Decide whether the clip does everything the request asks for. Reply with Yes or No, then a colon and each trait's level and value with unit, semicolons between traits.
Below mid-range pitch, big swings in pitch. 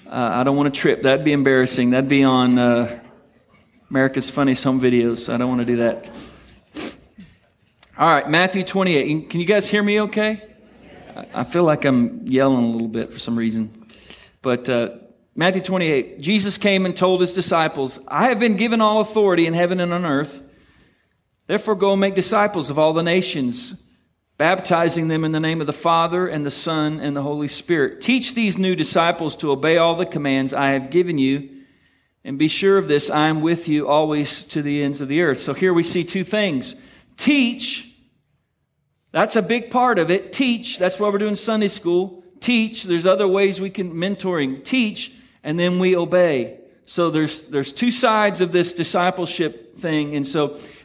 No: medium, 170 Hz; wide, 6.0 semitones